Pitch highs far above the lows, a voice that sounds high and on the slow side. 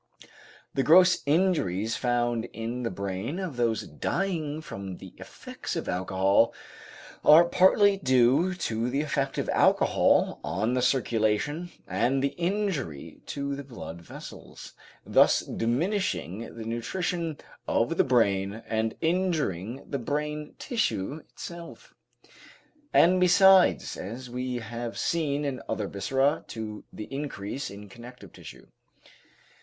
No: wide, 6.5 semitones; low, 125 Hz; slow, 125 wpm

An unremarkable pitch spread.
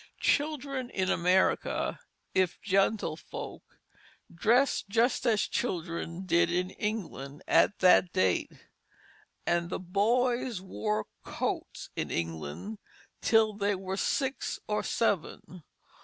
Yes: average, 4.6 semitones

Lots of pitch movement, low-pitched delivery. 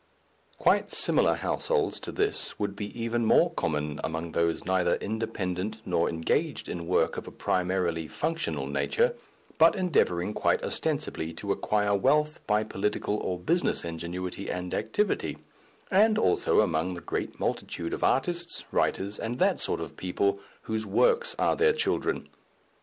Yes: wide, 9.0 semitones; low, 100 Hz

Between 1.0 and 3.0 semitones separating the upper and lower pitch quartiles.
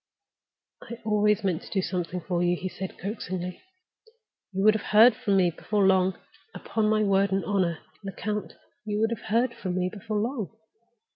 Yes: narrow, 2.6 semitones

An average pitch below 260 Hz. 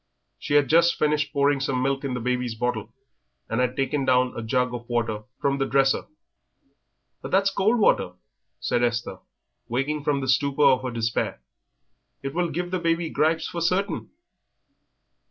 Yes: low, 135 Hz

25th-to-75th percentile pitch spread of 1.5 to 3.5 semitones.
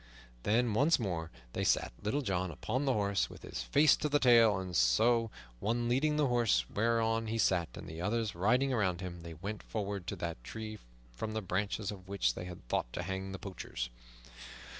No: average, 4.6 semitones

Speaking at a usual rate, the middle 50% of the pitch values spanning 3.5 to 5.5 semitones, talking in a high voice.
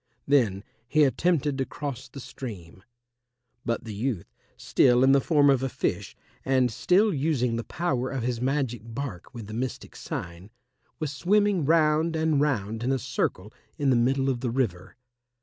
No: average, 170 wpm; average, 4.0 semitones; low, 130 Hz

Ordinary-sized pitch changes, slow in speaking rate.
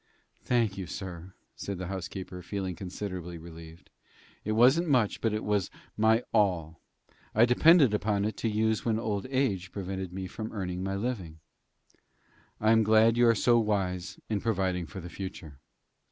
No: average, 3.4 semitones; average, 165 wpm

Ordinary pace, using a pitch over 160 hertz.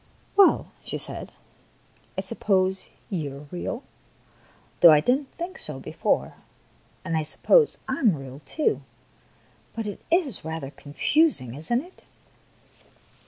Yes: average, 150 wpm; high, 190 Hz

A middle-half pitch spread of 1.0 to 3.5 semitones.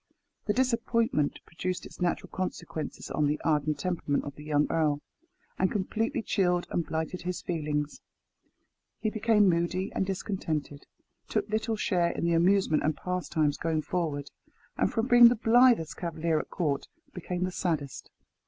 No: average, 4.6 semitones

